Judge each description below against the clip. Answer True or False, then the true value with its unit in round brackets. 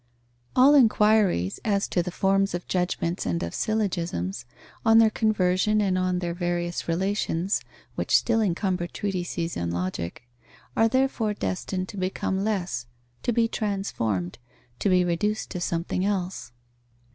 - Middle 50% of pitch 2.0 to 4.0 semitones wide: True (3.5 semitones)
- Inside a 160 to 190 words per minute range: False (145 wpm)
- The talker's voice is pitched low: False (185 Hz)